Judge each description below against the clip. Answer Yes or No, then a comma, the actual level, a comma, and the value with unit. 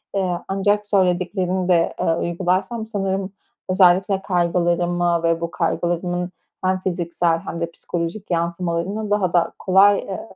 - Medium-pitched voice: Yes, medium, 180 Hz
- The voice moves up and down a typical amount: No, narrow, 2.0 semitones